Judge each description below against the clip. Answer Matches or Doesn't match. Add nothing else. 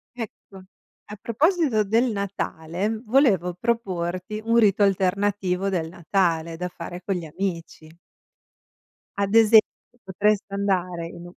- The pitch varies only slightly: Doesn't match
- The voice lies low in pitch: Doesn't match